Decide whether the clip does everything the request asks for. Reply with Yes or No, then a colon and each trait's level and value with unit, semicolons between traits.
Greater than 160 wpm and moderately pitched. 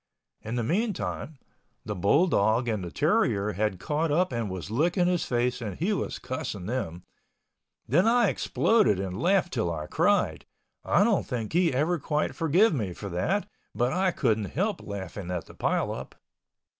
No: average, 170 wpm; low, 125 Hz